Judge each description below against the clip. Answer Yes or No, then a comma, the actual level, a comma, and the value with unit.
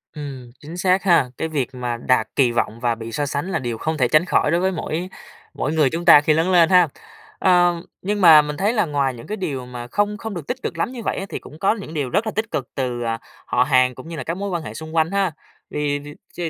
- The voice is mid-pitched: Yes, medium, 155 Hz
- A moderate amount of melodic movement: No, wide, 5.7 semitones